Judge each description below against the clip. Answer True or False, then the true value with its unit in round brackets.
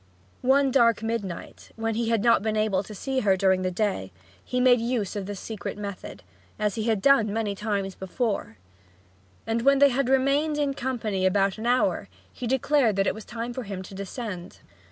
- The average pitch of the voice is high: True (220 Hz)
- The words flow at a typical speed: True (195 wpm)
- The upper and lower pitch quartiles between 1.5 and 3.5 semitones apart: False (4.0 semitones)